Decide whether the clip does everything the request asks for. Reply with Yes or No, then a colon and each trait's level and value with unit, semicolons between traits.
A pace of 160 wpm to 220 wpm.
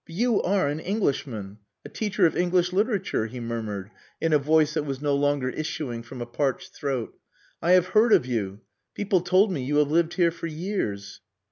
Yes: average, 200 wpm